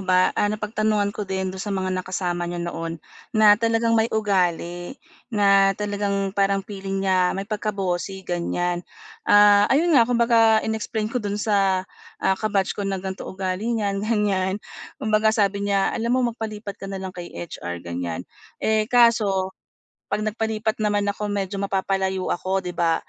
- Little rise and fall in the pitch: Yes, narrow, 2.3 semitones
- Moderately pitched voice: No, high, 200 Hz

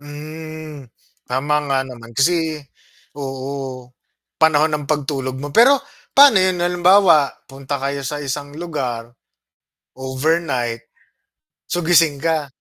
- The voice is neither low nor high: Yes, medium, 145 Hz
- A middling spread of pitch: Yes, average, 3.2 semitones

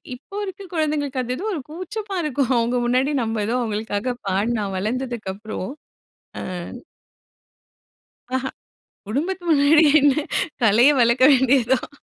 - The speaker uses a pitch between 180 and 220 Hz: No, very high, 255 Hz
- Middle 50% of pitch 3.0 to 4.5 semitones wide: No, average, 5.0 semitones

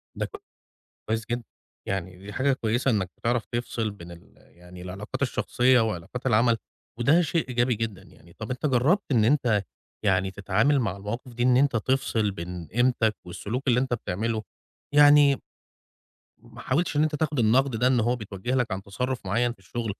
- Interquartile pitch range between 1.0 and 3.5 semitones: No, average, 4.2 semitones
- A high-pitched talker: No, low, 120 Hz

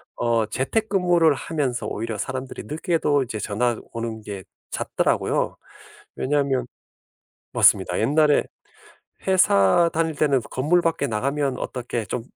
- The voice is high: No, low, 135 Hz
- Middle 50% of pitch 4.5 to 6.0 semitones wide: Yes, average, 5.3 semitones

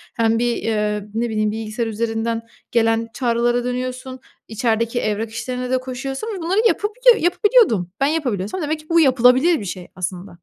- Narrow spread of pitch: No, average, 3.3 semitones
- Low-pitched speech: No, high, 240 Hz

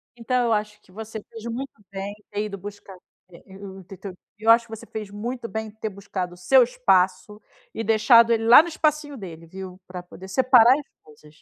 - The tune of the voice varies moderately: Yes, average, 3.5 semitones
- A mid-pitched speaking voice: No, high, 215 Hz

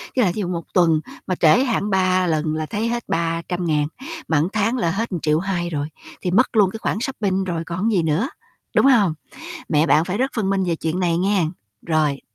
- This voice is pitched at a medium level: Yes, medium, 180 Hz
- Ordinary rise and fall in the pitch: Yes, average, 3.9 semitones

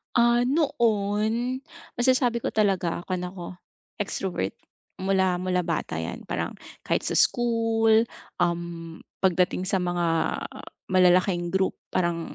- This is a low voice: No, high, 190 Hz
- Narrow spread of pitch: No, average, 4.5 semitones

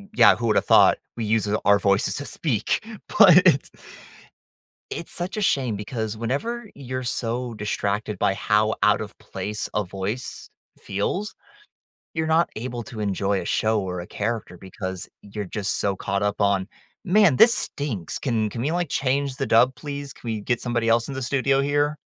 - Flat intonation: No, average, 5.3 semitones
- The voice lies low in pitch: Yes, low, 115 Hz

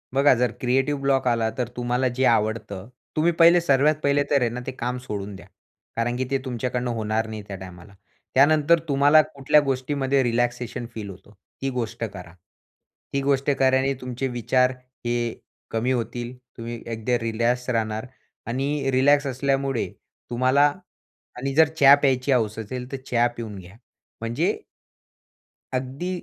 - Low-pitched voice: Yes, low, 125 Hz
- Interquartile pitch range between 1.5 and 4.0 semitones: Yes, average, 3.0 semitones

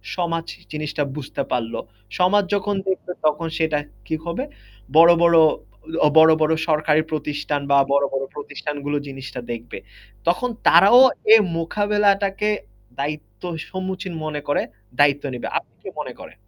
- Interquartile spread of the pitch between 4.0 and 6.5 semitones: Yes, average, 4.5 semitones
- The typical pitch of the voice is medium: Yes, medium, 155 Hz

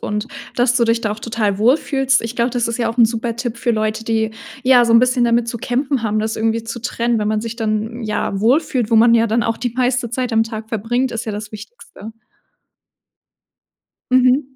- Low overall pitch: No, high, 230 Hz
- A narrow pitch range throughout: Yes, narrow, 1.8 semitones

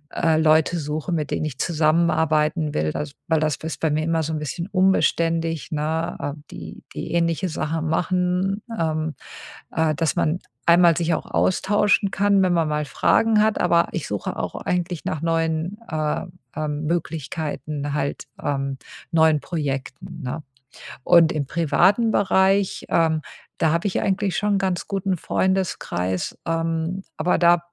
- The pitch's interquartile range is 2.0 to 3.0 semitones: Yes, narrow, 2.6 semitones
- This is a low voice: No, medium, 165 Hz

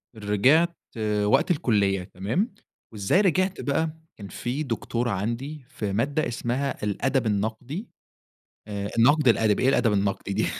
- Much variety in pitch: Yes, wide, 5.9 semitones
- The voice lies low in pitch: Yes, low, 120 Hz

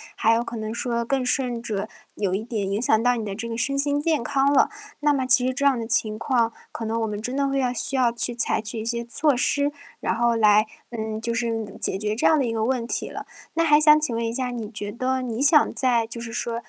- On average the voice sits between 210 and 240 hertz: Yes, high, 235 Hz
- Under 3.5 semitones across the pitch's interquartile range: Yes, average, 2.7 semitones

